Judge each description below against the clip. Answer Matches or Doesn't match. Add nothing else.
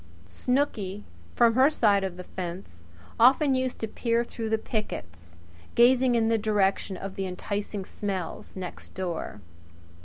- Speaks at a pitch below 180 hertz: Doesn't match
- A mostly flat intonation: Doesn't match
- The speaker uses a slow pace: Doesn't match